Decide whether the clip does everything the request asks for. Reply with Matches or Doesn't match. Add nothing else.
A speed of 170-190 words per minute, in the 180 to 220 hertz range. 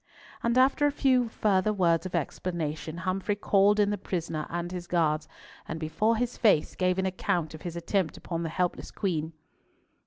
Matches